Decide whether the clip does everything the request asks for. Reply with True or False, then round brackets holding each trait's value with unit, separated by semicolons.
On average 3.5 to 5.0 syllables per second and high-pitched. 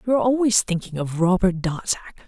False (5.8 syllables/s; 195 Hz)